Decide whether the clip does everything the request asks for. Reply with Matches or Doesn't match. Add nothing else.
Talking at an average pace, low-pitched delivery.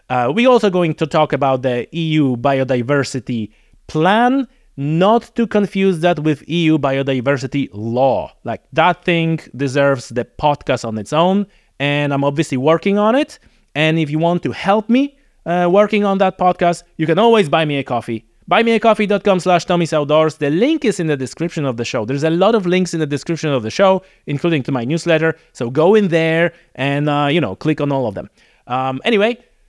Doesn't match